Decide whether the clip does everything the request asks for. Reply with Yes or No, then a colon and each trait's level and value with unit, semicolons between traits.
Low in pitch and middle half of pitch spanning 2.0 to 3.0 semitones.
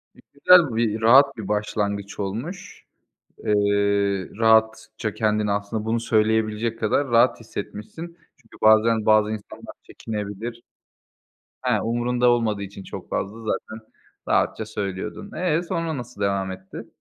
Yes: low, 110 Hz; narrow, 2.4 semitones